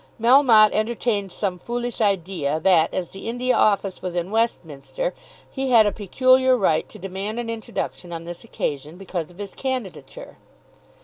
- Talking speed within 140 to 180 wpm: Yes, average, 160 wpm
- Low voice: No, high, 205 Hz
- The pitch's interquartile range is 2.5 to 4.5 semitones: No, average, 5.1 semitones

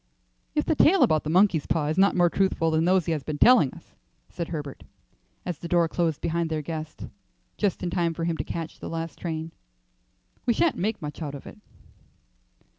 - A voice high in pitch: No, medium, 165 Hz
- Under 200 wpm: No, fast, 205 wpm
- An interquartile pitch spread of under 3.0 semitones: Yes, narrow, 2.4 semitones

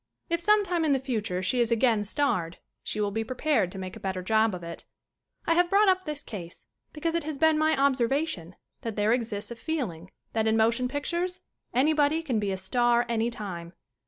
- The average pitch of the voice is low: No, high, 240 Hz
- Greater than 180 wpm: Yes, average, 200 wpm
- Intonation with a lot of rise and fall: Yes, wide, 6.9 semitones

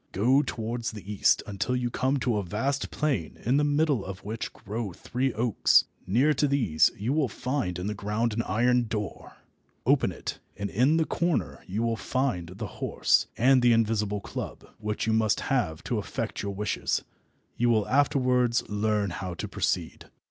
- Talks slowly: No, average, 180 wpm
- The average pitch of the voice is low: Yes, low, 115 Hz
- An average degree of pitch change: Yes, average, 3.9 semitones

